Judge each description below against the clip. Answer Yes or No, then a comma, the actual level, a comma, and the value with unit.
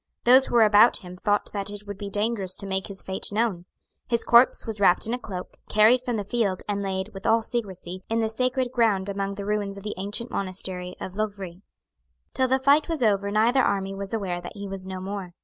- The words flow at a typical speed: No, fast, 230 wpm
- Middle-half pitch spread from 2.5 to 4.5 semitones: Yes, average, 3.0 semitones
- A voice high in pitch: Yes, high, 205 Hz